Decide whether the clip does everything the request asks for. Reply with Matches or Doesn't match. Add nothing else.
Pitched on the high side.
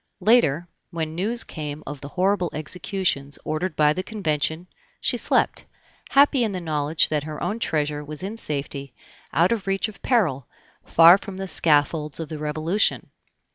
Doesn't match